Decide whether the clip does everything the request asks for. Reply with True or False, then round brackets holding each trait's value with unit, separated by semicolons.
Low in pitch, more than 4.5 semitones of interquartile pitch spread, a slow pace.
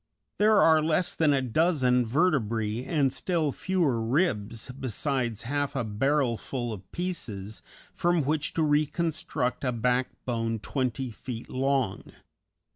True (130 Hz; 4.9 semitones; 120 wpm)